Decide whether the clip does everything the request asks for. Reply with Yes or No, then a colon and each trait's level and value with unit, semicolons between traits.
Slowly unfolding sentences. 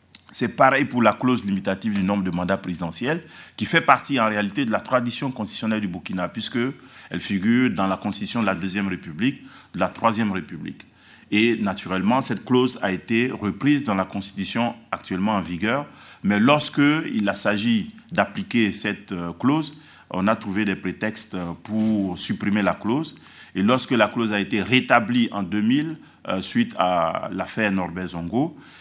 No: average, 165 wpm